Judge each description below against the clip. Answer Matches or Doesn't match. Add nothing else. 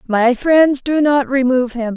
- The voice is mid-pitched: Doesn't match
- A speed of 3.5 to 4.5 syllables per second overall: Matches